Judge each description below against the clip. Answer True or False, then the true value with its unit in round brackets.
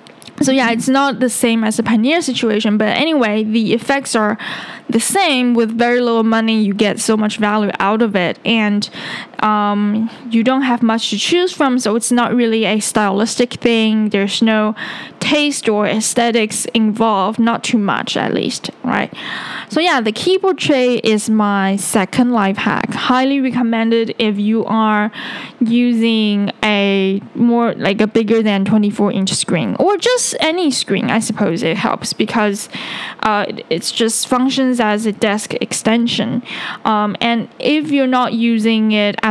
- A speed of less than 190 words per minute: True (165 wpm)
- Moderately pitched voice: False (225 Hz)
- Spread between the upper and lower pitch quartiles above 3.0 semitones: False (2.4 semitones)